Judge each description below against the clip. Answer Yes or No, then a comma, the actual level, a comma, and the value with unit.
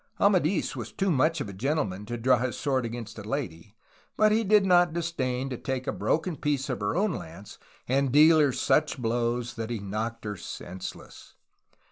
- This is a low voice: Yes, low, 130 Hz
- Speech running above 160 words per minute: Yes, average, 185 wpm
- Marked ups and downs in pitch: Yes, wide, 5.8 semitones